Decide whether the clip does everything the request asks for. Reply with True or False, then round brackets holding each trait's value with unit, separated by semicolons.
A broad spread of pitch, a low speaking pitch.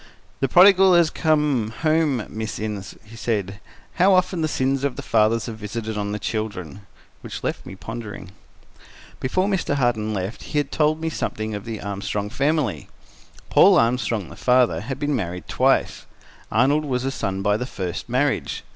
True (5.7 semitones; 115 Hz)